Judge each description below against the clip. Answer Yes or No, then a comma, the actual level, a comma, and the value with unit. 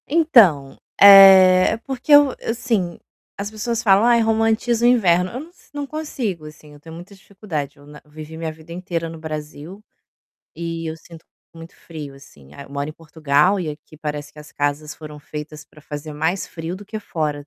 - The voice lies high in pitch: No, medium, 165 Hz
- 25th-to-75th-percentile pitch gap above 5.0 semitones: Yes, wide, 5.5 semitones